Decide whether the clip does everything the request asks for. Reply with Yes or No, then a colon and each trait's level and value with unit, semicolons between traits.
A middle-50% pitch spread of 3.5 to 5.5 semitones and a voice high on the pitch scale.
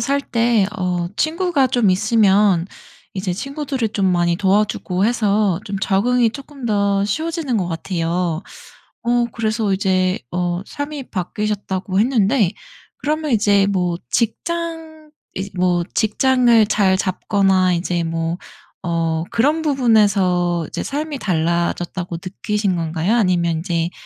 Yes: average, 5.1 semitones; high, 200 Hz